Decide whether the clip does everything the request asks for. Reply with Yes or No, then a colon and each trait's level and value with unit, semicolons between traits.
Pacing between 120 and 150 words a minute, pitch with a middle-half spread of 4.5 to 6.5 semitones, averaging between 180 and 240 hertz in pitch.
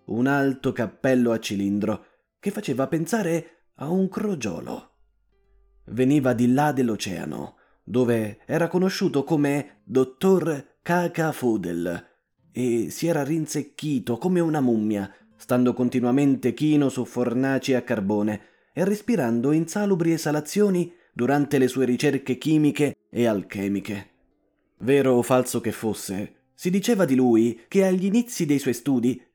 No: average, 125 wpm; wide, 5.6 semitones; low, 135 Hz